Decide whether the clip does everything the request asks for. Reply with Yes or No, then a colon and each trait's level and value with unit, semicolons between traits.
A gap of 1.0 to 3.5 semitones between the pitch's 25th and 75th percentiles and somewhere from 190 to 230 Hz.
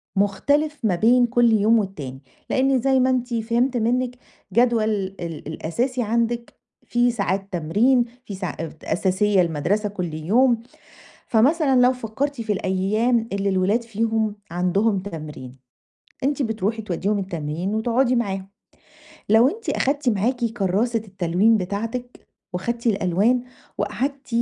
No: average, 4.2 semitones; high, 220 Hz